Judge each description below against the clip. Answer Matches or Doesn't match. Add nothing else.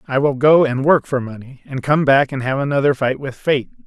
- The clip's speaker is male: Matches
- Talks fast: Matches